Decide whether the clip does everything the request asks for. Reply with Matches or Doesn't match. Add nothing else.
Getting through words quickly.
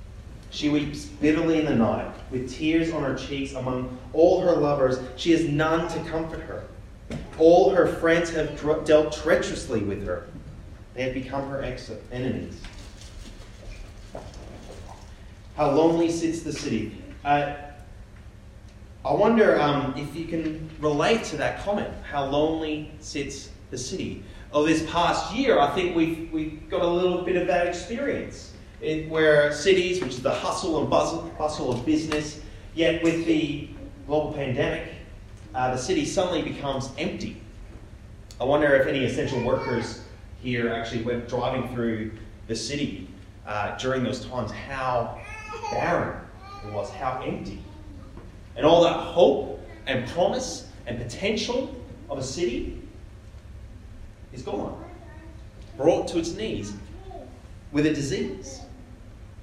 Doesn't match